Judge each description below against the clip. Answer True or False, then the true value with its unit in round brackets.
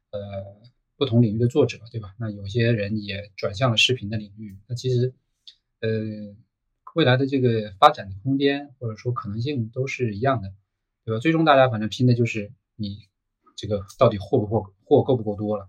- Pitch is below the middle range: True (110 Hz)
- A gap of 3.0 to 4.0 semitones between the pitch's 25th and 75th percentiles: True (3.4 semitones)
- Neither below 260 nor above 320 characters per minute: True (285 characters per minute)